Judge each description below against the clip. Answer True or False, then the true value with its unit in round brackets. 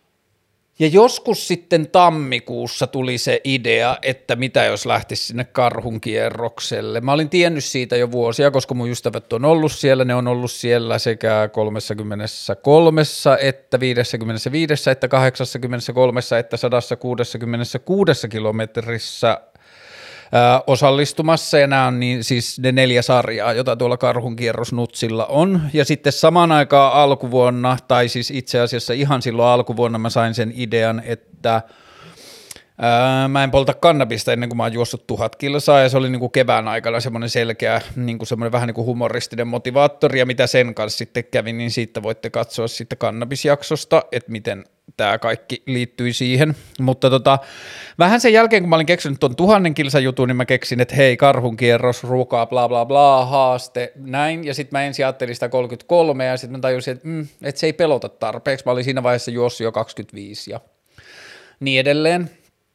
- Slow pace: False (155 wpm)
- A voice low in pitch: True (125 Hz)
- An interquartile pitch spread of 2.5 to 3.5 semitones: True (2.9 semitones)